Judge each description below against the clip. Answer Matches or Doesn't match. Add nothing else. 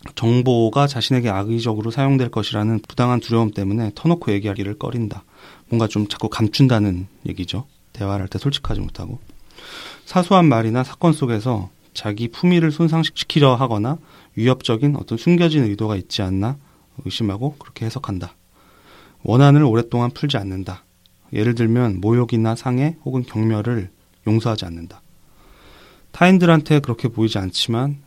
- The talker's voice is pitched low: Matches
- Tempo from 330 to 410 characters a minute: Matches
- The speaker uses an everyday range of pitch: Matches